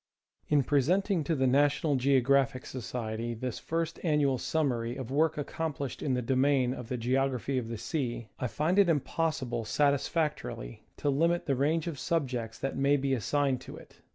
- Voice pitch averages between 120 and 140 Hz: Yes, low, 135 Hz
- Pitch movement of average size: Yes, average, 3.2 semitones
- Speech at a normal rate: Yes, average, 180 wpm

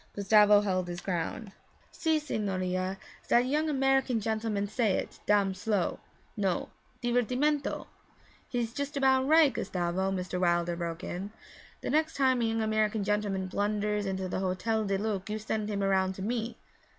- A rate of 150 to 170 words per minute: Yes, average, 155 wpm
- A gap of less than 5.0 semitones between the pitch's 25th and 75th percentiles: Yes, average, 4.1 semitones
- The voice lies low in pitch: No, high, 210 Hz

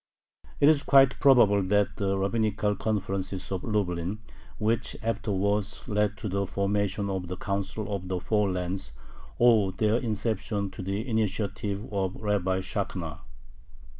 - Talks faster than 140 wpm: No, slow, 135 wpm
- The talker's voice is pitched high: No, low, 100 Hz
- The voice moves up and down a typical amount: No, narrow, 2.1 semitones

